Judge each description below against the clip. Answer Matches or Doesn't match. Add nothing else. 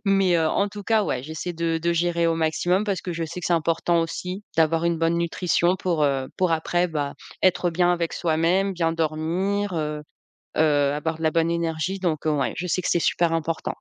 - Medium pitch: Matches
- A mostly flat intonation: Matches